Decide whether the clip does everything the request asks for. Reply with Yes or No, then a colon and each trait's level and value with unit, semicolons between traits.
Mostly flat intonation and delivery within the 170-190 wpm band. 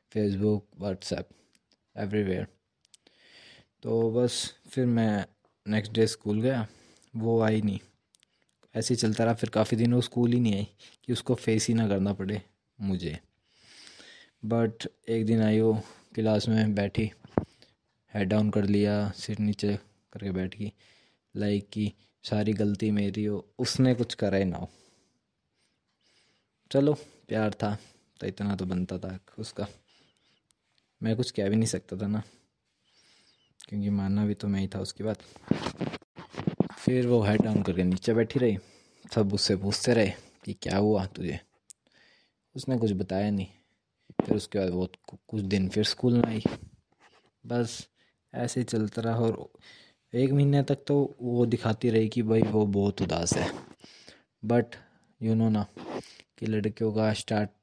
No: narrow, 2.3 semitones; average, 150 wpm